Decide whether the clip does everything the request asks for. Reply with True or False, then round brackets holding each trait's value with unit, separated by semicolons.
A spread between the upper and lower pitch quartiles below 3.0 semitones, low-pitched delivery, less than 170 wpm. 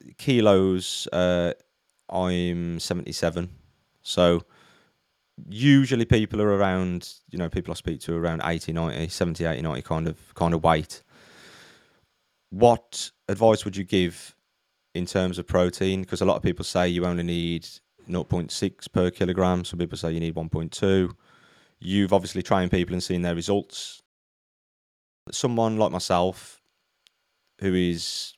True (2.4 semitones; 90 Hz; 140 wpm)